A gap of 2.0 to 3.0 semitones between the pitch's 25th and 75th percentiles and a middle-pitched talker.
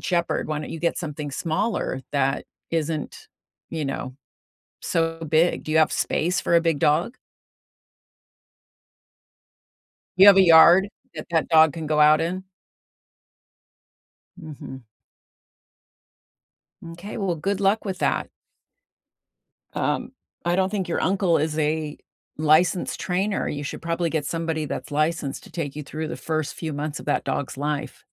Yes: narrow, 2.6 semitones; medium, 160 Hz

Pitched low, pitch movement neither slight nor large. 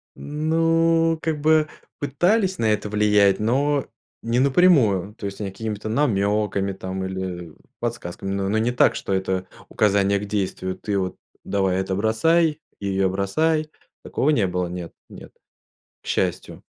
No: low, 105 Hz; wide, 7.3 semitones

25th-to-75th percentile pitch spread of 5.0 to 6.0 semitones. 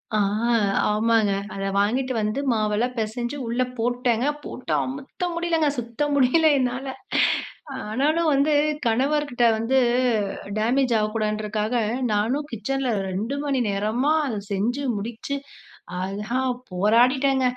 No: average, 4.1 semitones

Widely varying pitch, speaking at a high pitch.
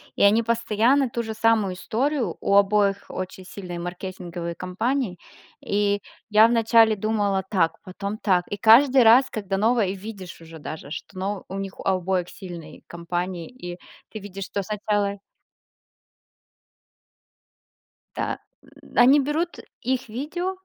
No: average, 3.6 semitones; high, 200 Hz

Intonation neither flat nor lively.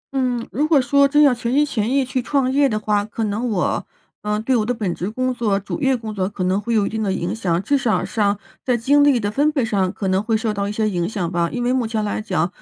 Yes: average, 4.0 semitones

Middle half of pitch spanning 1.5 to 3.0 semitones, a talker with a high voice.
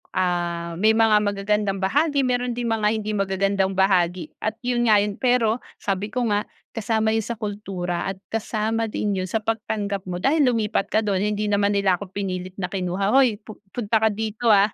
Yes: narrow, 2.5 semitones; high, 210 Hz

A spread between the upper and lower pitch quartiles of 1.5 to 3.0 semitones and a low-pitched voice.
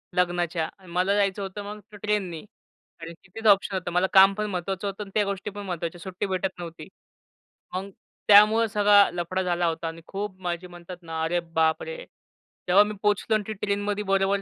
No: average, 2.7 semitones; high, 190 Hz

